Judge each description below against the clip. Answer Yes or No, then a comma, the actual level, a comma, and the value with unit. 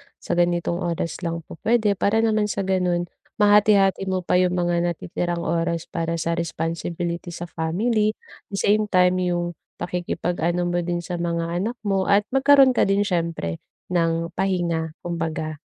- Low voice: No, medium, 175 Hz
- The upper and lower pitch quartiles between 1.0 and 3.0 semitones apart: Yes, narrow, 2.6 semitones